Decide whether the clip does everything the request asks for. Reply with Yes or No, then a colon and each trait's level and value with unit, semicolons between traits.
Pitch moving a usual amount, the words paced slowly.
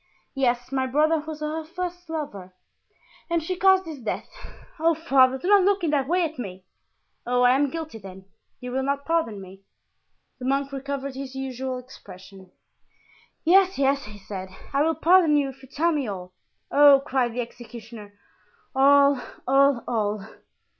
No: average, 4.6 semitones; average, 165 wpm